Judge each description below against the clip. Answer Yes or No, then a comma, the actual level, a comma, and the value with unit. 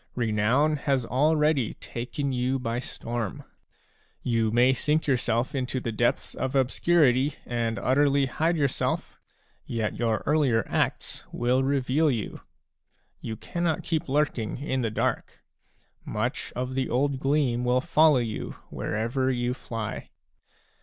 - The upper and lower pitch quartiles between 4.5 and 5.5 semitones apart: No, average, 3.2 semitones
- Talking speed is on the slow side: Yes, slow, 130 wpm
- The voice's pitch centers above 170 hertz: No, low, 130 Hz